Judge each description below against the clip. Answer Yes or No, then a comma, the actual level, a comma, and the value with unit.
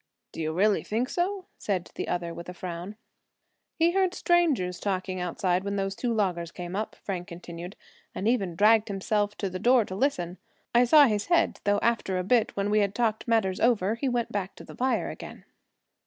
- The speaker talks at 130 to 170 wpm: No, average, 200 wpm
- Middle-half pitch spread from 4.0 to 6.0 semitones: Yes, average, 4.4 semitones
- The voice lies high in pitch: Yes, high, 205 Hz